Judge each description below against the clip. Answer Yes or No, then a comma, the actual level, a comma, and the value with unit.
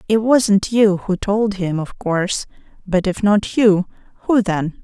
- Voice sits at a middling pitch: No, high, 200 Hz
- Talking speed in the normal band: Yes, average, 175 wpm